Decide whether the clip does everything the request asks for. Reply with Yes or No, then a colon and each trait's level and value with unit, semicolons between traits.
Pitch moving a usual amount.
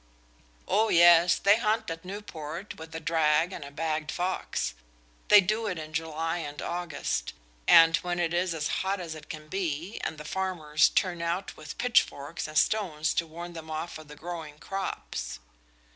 Yes: average, 3.0 semitones